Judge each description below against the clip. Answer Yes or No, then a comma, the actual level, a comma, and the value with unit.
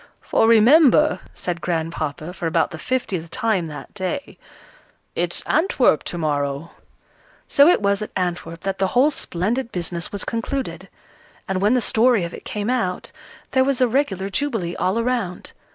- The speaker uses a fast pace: No, average, 160 wpm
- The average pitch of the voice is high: Yes, high, 195 Hz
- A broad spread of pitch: Yes, wide, 6.4 semitones